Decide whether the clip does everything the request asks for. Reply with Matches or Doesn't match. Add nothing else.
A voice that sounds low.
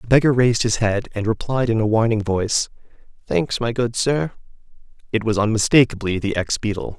Matches